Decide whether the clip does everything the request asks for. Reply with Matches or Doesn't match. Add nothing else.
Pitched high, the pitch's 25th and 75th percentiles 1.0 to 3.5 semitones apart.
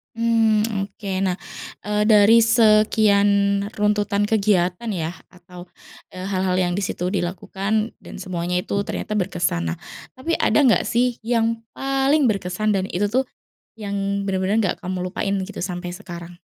Matches